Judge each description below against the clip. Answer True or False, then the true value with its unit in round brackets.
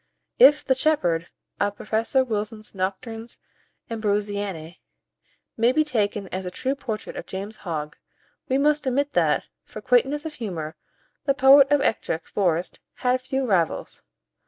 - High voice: True (225 Hz)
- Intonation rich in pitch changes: True (5.9 semitones)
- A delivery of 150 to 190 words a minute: False (140 wpm)